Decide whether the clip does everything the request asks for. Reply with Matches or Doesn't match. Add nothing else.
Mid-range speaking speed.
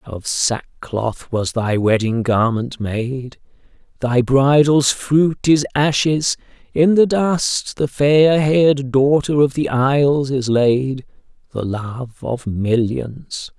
Doesn't match